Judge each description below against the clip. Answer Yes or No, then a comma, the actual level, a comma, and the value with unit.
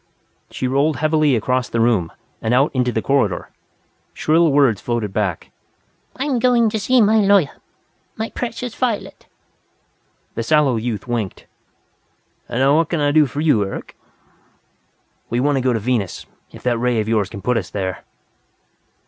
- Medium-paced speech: Yes, average, 165 wpm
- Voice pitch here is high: No, low, 130 Hz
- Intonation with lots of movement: Yes, wide, 5.7 semitones